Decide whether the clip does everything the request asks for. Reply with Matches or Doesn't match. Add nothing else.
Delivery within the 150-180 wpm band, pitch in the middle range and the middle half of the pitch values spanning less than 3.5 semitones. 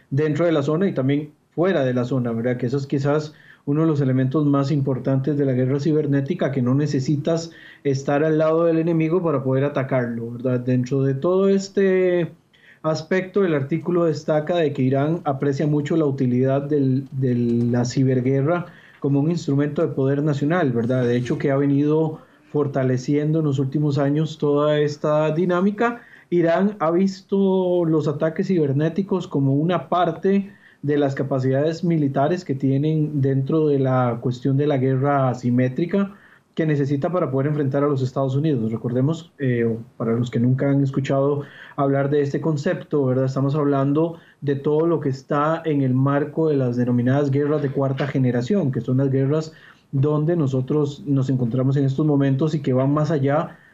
Matches